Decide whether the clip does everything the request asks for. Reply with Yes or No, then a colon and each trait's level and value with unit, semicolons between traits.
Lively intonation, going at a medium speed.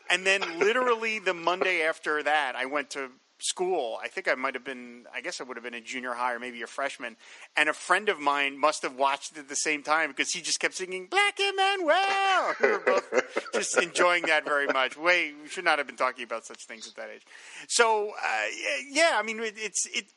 No: wide, 7.8 semitones; fast, 235 wpm